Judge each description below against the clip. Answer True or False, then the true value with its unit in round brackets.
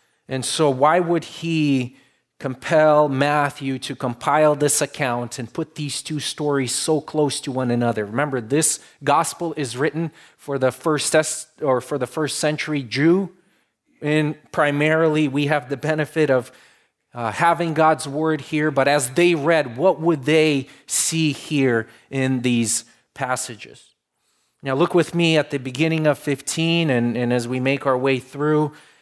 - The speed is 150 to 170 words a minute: True (155 wpm)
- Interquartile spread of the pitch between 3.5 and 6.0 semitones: False (2.9 semitones)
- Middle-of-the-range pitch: True (145 Hz)